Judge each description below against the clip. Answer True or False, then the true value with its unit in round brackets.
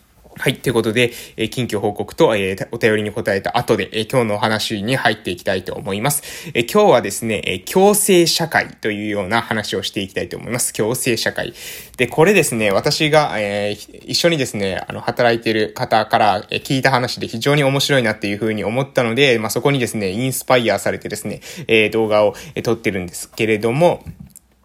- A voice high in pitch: False (115 Hz)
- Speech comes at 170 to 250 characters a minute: False (375 characters per minute)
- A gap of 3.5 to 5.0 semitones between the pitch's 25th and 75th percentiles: True (4.1 semitones)